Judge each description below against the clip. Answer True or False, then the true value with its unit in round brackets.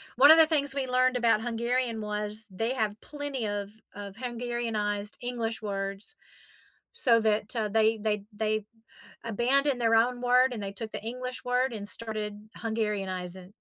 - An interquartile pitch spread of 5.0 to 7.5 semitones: False (3.0 semitones)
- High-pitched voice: True (225 Hz)